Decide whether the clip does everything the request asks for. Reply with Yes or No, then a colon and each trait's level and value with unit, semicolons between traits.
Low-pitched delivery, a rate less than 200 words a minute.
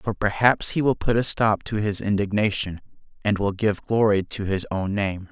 No: low, 105 Hz; fast, 205 wpm